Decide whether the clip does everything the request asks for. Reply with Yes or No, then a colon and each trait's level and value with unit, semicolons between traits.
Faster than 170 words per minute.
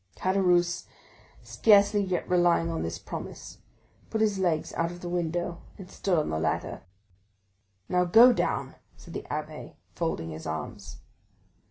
No: average, 145 wpm